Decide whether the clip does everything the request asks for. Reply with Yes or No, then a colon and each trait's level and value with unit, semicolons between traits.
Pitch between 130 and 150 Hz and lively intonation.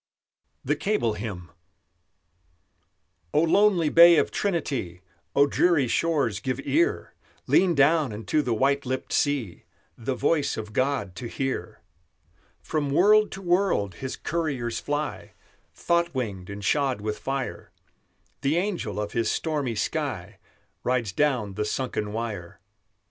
Yes: low, 135 Hz; wide, 6.7 semitones